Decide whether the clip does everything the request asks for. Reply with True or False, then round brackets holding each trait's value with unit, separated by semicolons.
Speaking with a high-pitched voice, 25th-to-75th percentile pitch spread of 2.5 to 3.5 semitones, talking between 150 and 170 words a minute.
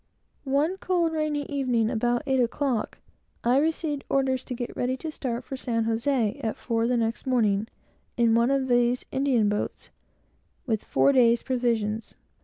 True (245 Hz; 3.0 semitones; 160 wpm)